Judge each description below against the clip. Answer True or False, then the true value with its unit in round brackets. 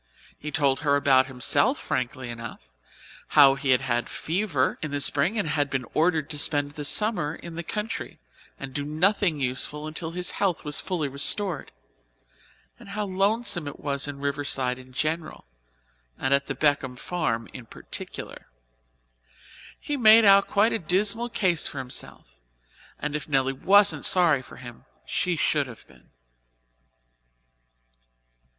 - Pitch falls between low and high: True (150 Hz)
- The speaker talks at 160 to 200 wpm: False (150 wpm)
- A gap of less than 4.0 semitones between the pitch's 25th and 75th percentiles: False (5.1 semitones)